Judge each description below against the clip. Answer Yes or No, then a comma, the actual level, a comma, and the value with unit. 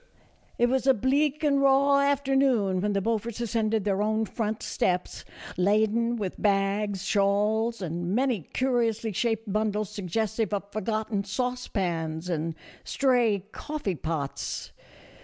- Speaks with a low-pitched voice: No, high, 215 Hz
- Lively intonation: No, average, 3.5 semitones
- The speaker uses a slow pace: Yes, slow, 130 wpm